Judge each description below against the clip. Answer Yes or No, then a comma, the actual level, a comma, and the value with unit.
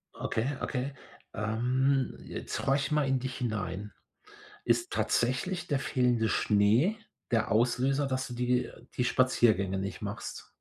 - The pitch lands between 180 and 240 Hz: No, low, 125 Hz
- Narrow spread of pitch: No, average, 3.5 semitones